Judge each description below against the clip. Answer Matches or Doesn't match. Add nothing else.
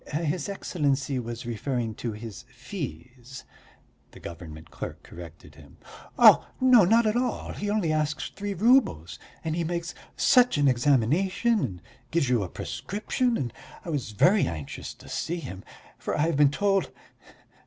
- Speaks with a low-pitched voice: Doesn't match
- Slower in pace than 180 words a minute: Matches